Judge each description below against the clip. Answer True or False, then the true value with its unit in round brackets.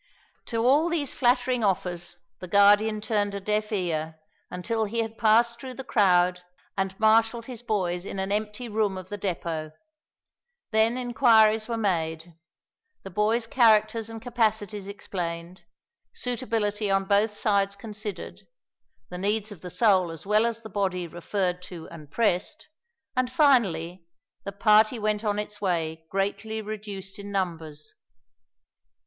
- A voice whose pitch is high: True (205 Hz)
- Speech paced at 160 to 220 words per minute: False (145 wpm)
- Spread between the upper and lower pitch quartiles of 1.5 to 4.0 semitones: True (3.5 semitones)